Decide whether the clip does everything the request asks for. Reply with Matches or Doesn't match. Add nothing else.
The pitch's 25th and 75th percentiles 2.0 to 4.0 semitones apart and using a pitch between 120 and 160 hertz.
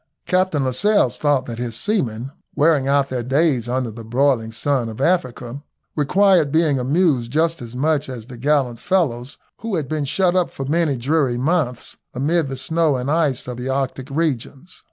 Doesn't match